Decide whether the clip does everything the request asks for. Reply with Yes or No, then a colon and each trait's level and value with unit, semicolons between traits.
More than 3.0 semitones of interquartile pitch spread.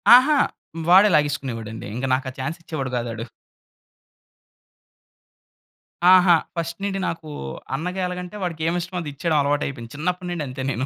Yes: average, 5.1 semitones